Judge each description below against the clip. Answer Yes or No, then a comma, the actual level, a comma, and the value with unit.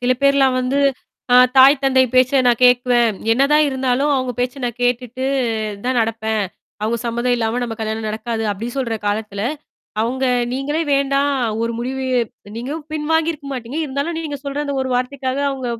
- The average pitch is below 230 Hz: No, very high, 255 Hz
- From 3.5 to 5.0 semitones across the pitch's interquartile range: No, average, 2.9 semitones